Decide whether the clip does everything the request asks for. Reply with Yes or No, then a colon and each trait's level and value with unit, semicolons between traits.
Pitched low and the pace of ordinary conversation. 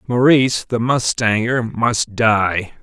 No: low, 115 Hz; slow, 105 wpm